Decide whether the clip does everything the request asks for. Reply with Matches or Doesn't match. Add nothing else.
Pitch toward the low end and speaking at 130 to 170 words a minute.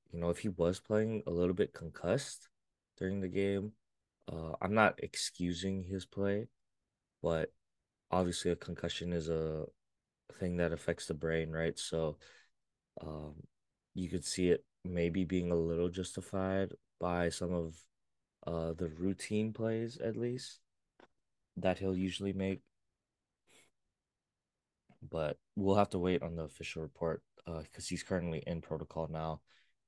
Matches